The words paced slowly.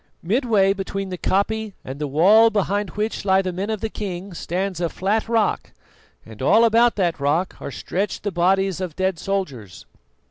No: average, 180 wpm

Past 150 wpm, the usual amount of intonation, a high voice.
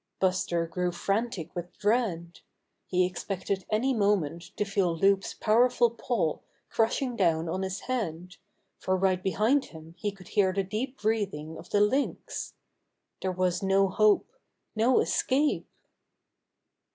No: average, 145 wpm; average, 3.5 semitones; high, 195 Hz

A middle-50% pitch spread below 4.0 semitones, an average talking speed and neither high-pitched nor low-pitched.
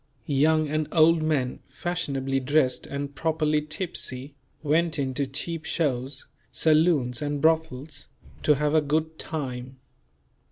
No: average, 2.7 semitones; slow, 125 wpm; medium, 150 Hz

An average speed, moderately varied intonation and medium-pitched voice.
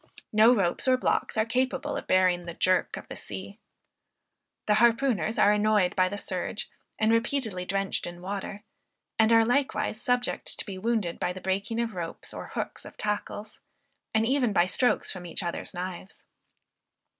No: average, 170 wpm; average, 3.7 semitones; high, 210 Hz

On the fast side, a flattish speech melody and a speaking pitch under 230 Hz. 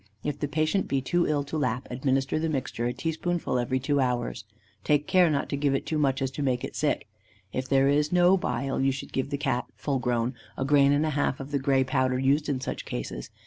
Yes: fast, 245 wpm; narrow, 2.3 semitones; medium, 140 Hz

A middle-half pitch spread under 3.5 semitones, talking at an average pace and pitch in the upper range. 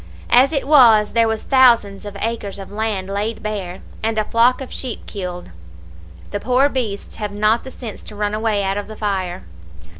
Yes: narrow, 2.5 semitones; average, 190 wpm; high, 215 Hz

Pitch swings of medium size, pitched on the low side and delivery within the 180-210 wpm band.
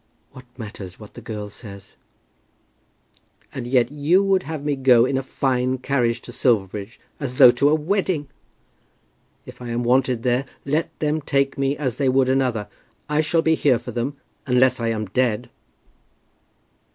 No: average, 3.4 semitones; low, 130 Hz; average, 165 wpm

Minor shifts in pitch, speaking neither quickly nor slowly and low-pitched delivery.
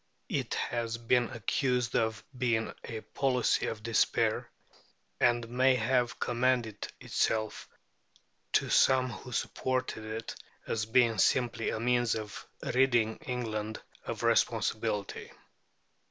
No: narrow, 2.1 semitones; slow, 110 wpm; low, 120 Hz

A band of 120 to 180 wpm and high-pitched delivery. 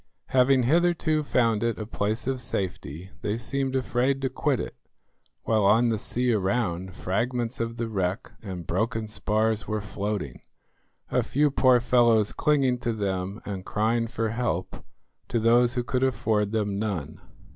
No: average, 155 wpm; low, 115 Hz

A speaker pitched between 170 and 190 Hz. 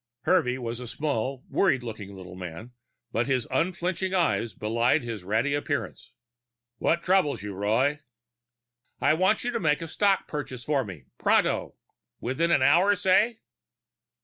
No: low, 135 Hz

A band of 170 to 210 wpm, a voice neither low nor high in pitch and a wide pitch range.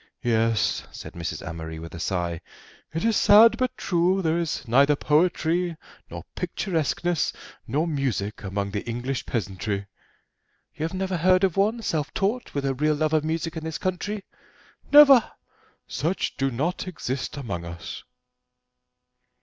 No: average, 150 wpm; medium, 155 Hz; wide, 8.1 semitones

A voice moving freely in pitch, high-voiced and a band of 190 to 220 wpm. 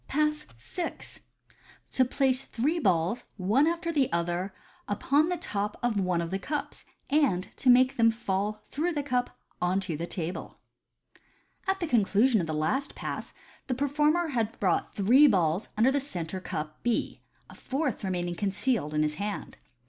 No: wide, 7.4 semitones; high, 225 Hz; average, 170 wpm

